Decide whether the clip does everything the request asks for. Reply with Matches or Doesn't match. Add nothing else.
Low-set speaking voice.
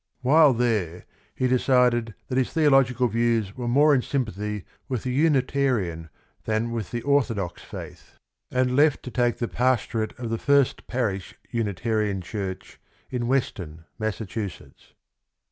Matches